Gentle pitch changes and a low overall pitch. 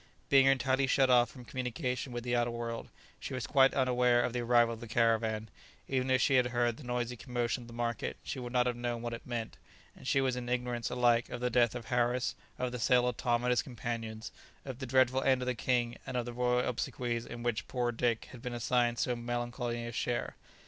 Yes: narrow, 1.1 semitones; low, 120 Hz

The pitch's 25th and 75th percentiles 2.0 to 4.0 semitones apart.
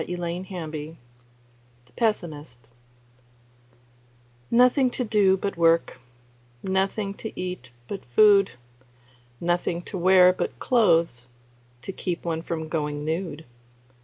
Yes: average, 3.6 semitones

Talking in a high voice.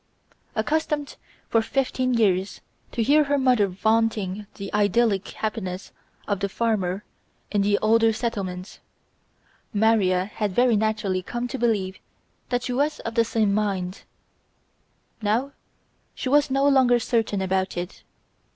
Yes: high, 220 Hz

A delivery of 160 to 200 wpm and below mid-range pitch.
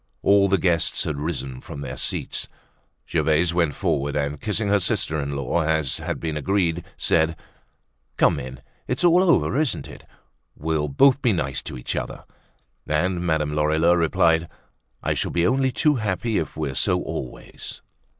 Yes: average, 165 wpm; very low, 80 Hz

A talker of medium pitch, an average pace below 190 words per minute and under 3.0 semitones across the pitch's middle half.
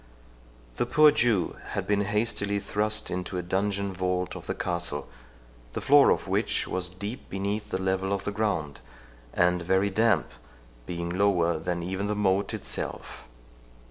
No: very low, 95 Hz; average, 155 wpm; narrow, 2.5 semitones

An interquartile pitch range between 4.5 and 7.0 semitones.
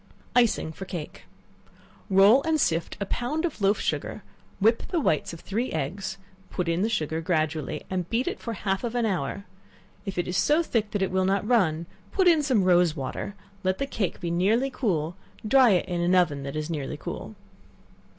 Yes: wide, 5.4 semitones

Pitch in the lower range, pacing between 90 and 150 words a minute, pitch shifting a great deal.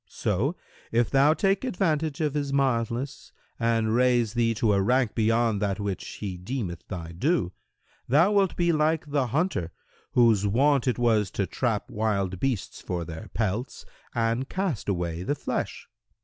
No: low, 115 Hz; average, 160 wpm; wide, 5.7 semitones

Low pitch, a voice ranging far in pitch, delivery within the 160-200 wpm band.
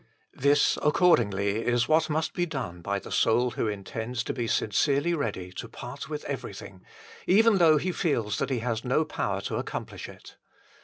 Yes: low, 125 Hz; wide, 6.2 semitones; average, 175 wpm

